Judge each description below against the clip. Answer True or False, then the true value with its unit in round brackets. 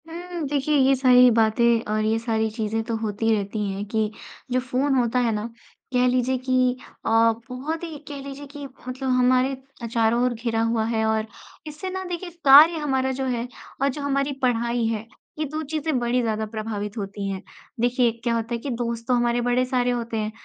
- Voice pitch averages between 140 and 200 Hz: False (245 Hz)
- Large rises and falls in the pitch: False (3.3 semitones)